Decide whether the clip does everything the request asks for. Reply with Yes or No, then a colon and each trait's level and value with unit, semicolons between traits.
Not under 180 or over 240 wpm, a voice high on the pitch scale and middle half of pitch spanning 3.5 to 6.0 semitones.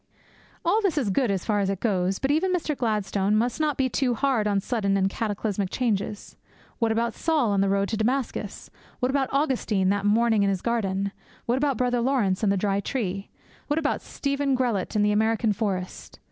Yes: average, 200 wpm; high, 220 Hz; average, 4.8 semitones